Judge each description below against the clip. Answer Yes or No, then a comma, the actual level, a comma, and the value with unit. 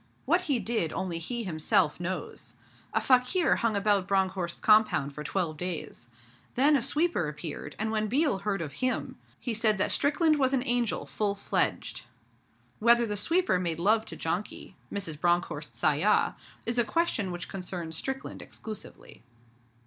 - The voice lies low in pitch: No, high, 205 Hz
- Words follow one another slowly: No, average, 155 wpm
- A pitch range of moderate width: No, wide, 5.7 semitones